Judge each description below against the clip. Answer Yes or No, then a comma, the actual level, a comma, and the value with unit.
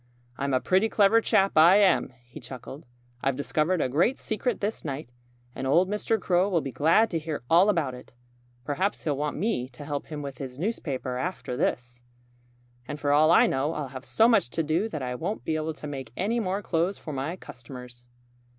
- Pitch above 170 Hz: No, medium, 155 Hz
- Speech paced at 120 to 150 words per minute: No, fast, 205 wpm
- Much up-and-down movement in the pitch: Yes, wide, 5.9 semitones